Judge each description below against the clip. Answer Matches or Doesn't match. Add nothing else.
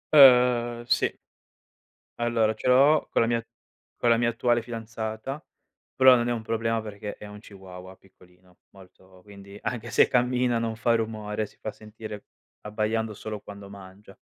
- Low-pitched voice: Matches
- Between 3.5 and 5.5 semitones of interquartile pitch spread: Doesn't match